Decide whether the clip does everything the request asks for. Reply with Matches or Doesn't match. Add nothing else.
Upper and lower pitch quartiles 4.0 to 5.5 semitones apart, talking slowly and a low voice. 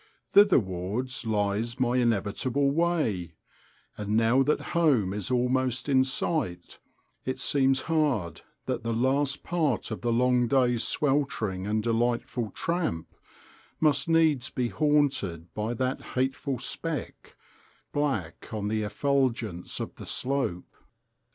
Matches